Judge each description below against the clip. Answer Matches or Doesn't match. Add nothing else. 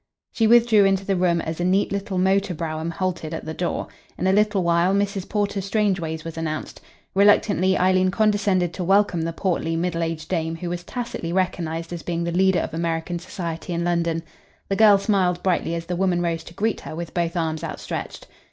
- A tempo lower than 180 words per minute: Doesn't match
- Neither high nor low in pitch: Matches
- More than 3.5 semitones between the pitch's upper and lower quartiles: Doesn't match